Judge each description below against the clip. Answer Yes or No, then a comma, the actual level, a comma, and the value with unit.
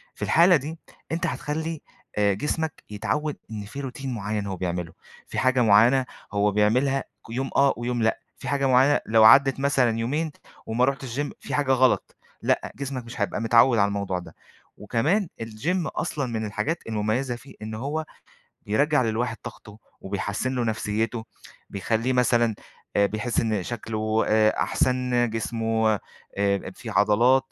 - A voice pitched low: Yes, low, 115 Hz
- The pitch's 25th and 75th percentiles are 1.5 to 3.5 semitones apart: No, average, 3.9 semitones